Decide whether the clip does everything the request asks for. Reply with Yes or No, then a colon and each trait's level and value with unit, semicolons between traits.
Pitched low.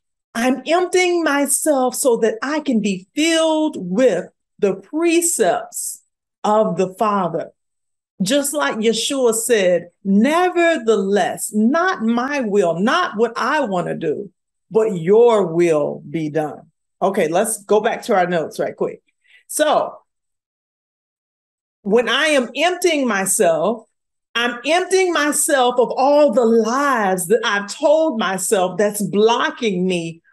No: high, 235 Hz